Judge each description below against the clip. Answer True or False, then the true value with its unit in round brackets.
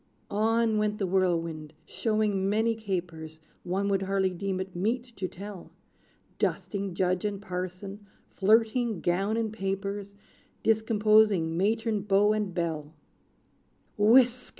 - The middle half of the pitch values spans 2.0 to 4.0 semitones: True (2.8 semitones)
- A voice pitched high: True (200 Hz)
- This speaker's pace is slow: True (120 wpm)